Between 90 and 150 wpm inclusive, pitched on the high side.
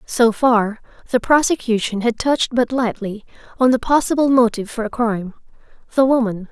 Yes: average, 145 wpm; high, 235 Hz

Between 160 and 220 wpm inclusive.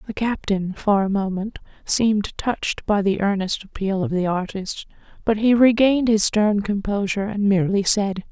Yes: average, 165 wpm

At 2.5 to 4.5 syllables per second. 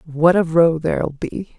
Yes: 4.1 syllables/s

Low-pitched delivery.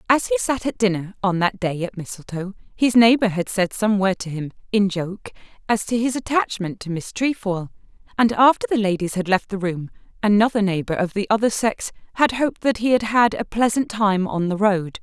No: high, 210 Hz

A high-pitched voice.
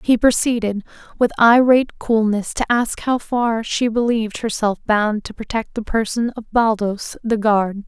Yes: high, 225 Hz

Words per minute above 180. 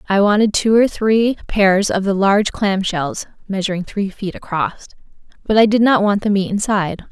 Yes: average, 195 wpm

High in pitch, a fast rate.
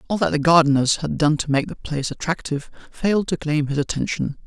No: medium, 150 Hz; fast, 215 wpm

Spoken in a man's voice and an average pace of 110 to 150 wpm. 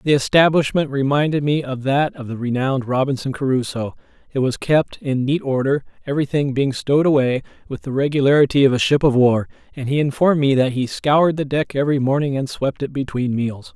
No: male; average, 195 wpm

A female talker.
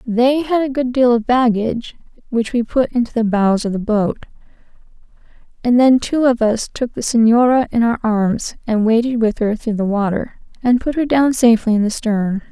Yes: female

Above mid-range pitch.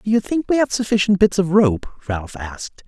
No: medium, 180 Hz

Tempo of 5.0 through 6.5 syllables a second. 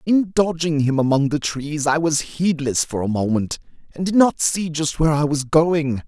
No: 4.6 syllables/s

